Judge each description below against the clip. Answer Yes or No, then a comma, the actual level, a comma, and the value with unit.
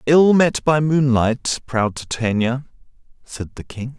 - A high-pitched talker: No, low, 130 Hz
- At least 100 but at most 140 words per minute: Yes, slow, 135 wpm